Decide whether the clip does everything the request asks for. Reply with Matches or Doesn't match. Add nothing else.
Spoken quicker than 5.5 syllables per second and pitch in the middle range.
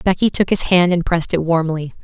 Matches